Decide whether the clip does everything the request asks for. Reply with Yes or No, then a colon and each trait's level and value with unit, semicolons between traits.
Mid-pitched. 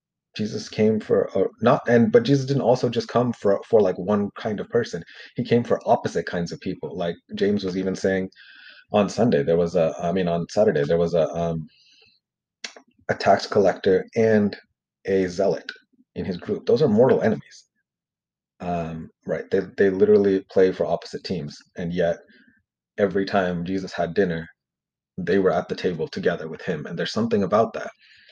No: very low, 95 Hz